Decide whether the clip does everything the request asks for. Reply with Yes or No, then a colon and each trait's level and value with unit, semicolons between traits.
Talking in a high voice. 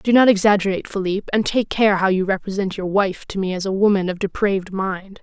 Yes: high, 195 Hz